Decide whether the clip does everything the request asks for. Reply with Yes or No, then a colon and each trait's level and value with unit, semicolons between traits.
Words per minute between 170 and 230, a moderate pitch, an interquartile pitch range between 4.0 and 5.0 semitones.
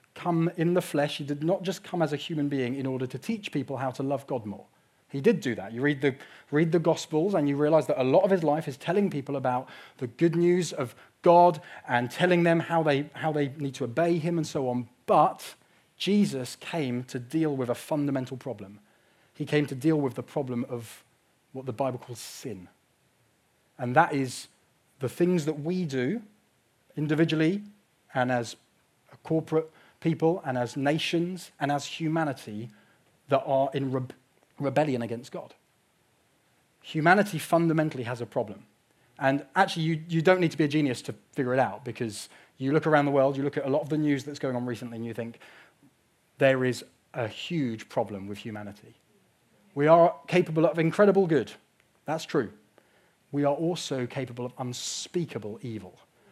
Yes: average, 190 wpm; medium, 145 Hz; average, 4.4 semitones